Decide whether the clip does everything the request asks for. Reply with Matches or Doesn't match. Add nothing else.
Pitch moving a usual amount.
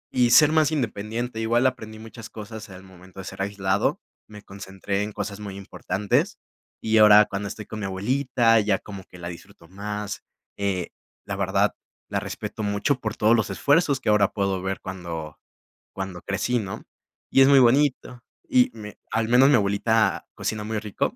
Matches